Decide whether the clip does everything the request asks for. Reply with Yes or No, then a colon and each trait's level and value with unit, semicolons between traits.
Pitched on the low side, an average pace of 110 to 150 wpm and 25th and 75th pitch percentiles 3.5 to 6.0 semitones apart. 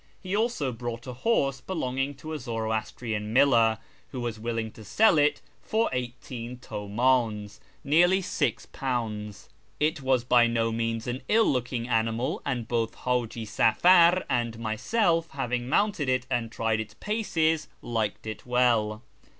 Yes: low, 125 Hz; average, 140 wpm; average, 4.0 semitones